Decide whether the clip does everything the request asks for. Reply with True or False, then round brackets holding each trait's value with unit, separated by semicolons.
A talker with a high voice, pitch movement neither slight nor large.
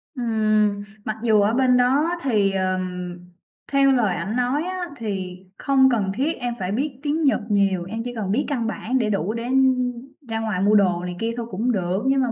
True (225 Hz; 4.7 semitones)